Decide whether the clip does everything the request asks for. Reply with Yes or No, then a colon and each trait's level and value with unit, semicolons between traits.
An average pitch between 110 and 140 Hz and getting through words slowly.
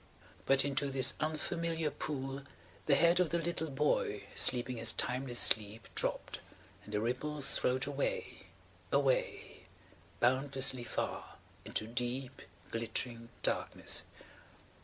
Yes: low, 135 Hz; slow, 100 wpm